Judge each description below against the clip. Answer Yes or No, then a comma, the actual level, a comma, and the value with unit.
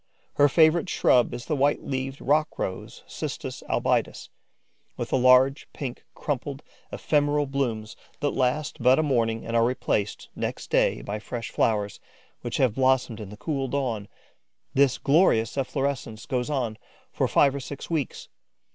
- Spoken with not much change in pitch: No, average, 3.6 semitones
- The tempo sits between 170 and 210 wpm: No, average, 155 wpm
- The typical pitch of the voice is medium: No, low, 130 Hz